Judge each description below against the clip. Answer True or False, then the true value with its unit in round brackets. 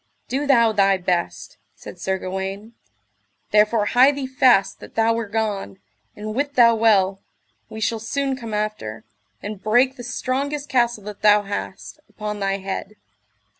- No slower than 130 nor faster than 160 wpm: True (155 wpm)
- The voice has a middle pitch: False (215 Hz)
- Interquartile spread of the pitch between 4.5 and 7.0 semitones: False (3.8 semitones)